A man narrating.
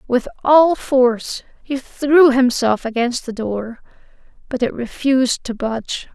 No: female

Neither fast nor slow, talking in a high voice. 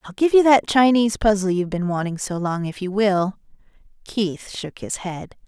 Yes: average, 195 wpm; high, 200 Hz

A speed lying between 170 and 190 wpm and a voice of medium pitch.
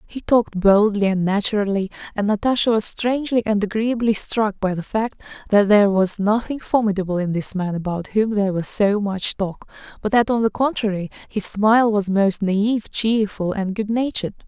No: average, 180 wpm; high, 210 Hz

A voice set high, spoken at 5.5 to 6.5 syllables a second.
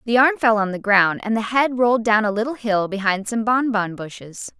No: high, 220 Hz; 5.3 syllables/s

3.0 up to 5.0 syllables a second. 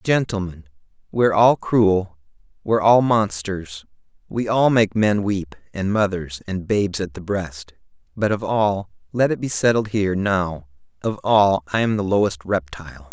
Yes: 4.5 syllables/s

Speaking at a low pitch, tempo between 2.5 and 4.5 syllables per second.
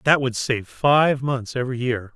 Yes: low, 125 Hz; 4.4 syllables/s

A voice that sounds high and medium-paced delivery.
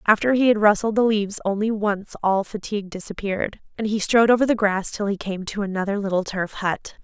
No: high, 205 Hz; fast, 215 wpm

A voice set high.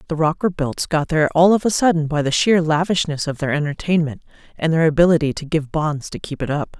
No: medium, 160 Hz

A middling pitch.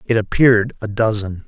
No: low, 110 Hz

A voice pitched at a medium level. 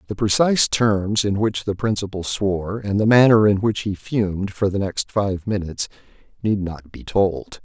No: low, 100 Hz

